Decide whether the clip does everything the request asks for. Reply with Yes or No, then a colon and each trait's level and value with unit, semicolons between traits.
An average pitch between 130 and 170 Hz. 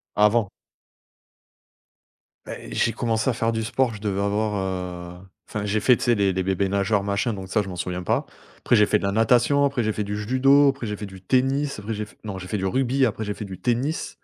No: low, 105 Hz